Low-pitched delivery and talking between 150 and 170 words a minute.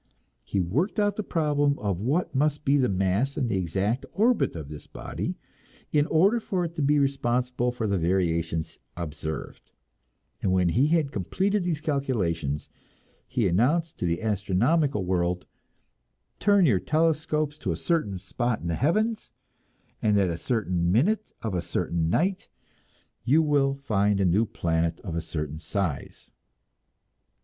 Yes: low, 120 Hz; average, 155 wpm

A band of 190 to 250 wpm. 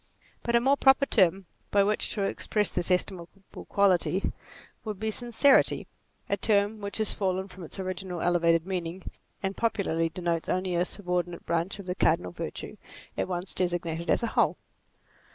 No: average, 170 wpm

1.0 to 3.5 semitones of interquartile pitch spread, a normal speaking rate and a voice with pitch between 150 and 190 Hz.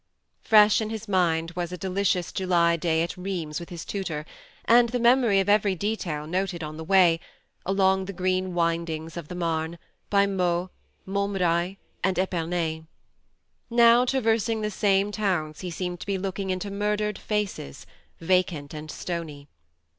Yes: average, 3.1 semitones; average, 155 wpm; medium, 185 Hz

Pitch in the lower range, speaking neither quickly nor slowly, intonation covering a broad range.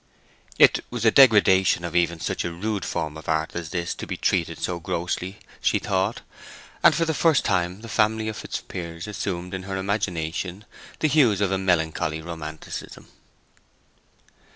No: very low, 95 Hz; average, 165 wpm; average, 3.9 semitones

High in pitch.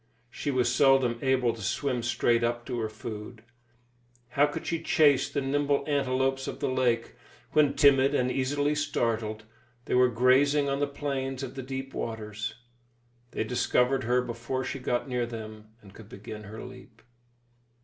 No: low, 125 Hz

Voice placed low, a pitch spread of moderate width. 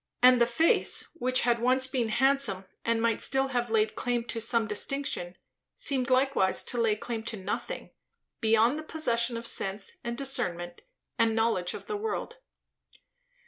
No: high, 235 Hz; average, 3.1 semitones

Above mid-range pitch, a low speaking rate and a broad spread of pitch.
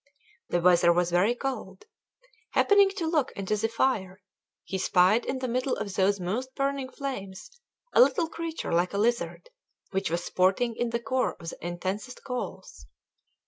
No: high, 220 Hz; average, 165 wpm; wide, 5.7 semitones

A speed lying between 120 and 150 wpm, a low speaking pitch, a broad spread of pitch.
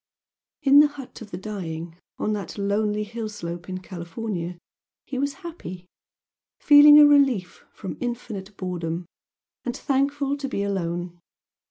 No: average, 140 wpm; high, 210 Hz; wide, 7.3 semitones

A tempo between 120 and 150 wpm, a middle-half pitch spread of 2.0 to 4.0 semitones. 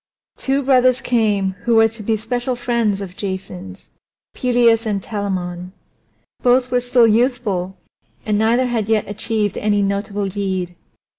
Yes: average, 140 wpm; average, 3.6 semitones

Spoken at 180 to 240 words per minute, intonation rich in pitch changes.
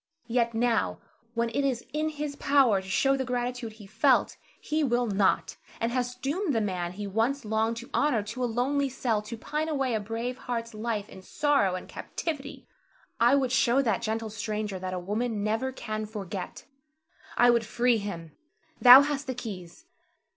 No: average, 185 wpm; average, 3.7 semitones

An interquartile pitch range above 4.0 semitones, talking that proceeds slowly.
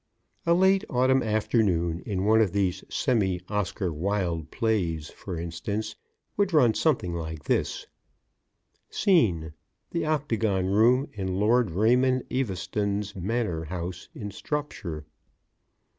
Yes: wide, 5.6 semitones; slow, 120 wpm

